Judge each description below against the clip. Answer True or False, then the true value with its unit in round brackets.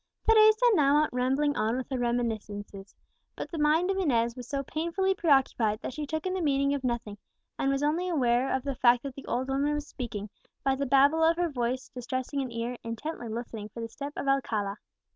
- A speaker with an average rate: False (215 wpm)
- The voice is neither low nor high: False (270 Hz)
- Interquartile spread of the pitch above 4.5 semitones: False (4.0 semitones)